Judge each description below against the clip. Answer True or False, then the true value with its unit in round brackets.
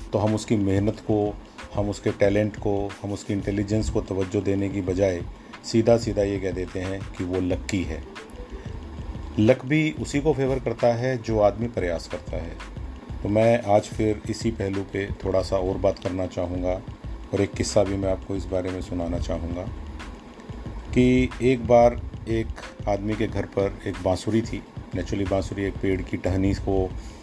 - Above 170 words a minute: True (180 wpm)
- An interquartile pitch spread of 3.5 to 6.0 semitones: False (2.9 semitones)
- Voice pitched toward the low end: True (100 Hz)